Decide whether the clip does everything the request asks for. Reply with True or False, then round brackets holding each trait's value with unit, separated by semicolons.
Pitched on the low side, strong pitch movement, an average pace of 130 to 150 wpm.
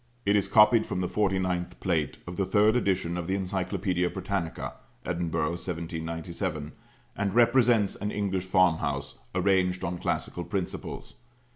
False (95 Hz; 2.5 semitones; 135 wpm)